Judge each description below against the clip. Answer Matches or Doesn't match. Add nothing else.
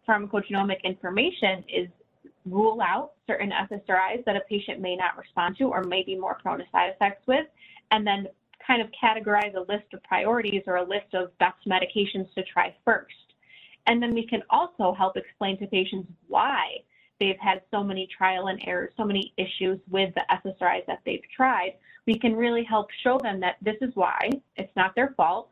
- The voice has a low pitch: Doesn't match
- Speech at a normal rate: Matches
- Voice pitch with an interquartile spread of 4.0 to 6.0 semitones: Doesn't match